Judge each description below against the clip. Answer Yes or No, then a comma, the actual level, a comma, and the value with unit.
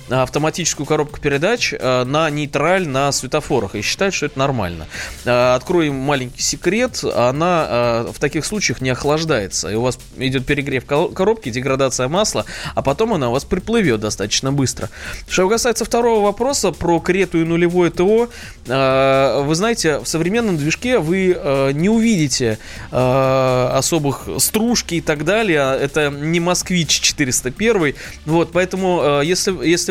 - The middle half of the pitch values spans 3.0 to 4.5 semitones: No, wide, 5.6 semitones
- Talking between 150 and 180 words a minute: No, average, 135 wpm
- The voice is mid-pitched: Yes, medium, 150 Hz